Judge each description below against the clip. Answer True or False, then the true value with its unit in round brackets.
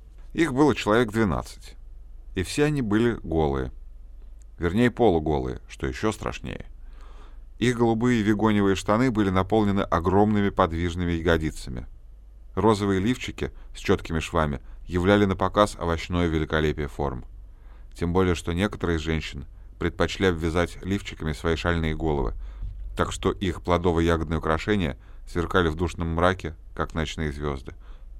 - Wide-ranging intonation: False (4.2 semitones)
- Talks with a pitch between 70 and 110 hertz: True (85 Hz)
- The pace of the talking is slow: False (125 wpm)